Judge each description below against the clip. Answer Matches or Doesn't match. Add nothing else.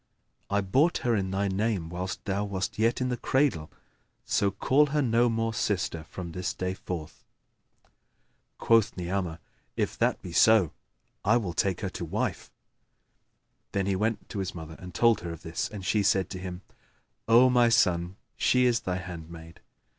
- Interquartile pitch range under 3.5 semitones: Doesn't match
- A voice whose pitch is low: Matches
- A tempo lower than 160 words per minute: Doesn't match